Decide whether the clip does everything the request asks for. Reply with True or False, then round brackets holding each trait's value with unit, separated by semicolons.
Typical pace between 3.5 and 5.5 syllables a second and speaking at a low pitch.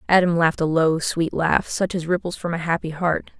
False (5.4 syllables/s; 170 Hz)